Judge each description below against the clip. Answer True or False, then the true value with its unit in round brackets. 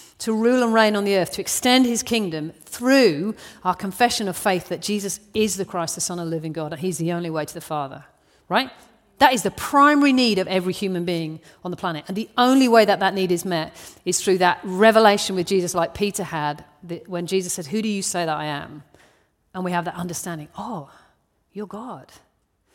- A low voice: False (185 Hz)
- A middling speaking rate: False (220 wpm)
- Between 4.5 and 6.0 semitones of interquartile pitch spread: False (3.7 semitones)